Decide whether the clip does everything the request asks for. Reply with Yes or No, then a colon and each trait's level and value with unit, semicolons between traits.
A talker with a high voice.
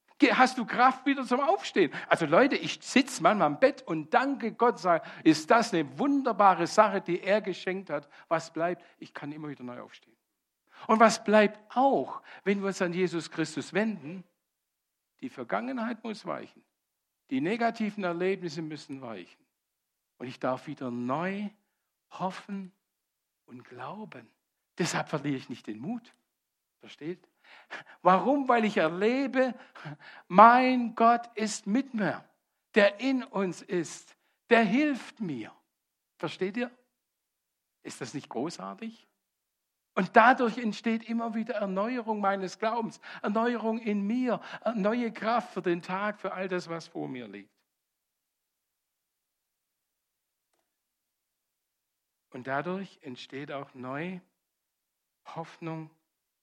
Yes: high, 200 Hz